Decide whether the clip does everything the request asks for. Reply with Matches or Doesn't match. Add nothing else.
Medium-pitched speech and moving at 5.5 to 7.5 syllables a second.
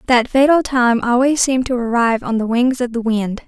Doesn't match